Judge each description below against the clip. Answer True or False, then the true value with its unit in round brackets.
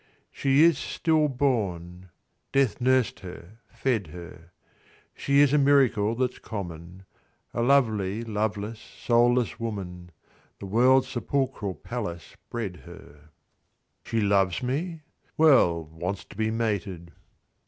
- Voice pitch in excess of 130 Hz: False (110 Hz)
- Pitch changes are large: True (5.9 semitones)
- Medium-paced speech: False (120 wpm)